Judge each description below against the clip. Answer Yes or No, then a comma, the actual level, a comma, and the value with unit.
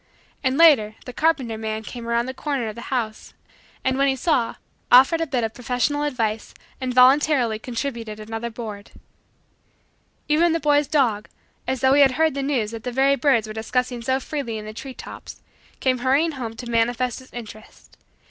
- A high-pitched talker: Yes, very high, 250 Hz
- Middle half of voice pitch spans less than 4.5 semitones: Yes, average, 3.5 semitones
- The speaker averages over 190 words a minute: No, average, 185 wpm